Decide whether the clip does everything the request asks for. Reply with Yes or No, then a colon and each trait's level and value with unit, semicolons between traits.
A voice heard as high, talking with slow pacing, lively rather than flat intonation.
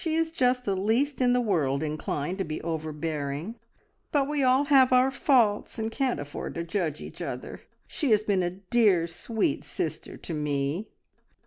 No: high, 205 Hz; average, 180 wpm; wide, 8.1 semitones